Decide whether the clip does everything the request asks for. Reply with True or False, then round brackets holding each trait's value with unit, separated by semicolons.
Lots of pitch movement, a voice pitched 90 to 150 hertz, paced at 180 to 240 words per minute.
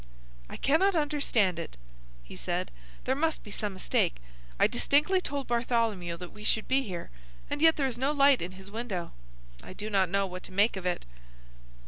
False (7.0 semitones; 220 Hz; 190 wpm)